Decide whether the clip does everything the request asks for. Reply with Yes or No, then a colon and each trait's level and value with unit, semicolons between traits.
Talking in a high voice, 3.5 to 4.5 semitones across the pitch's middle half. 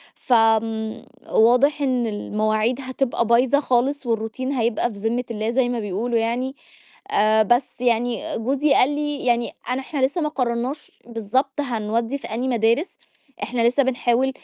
No: high, 240 Hz; average, 2.8 semitones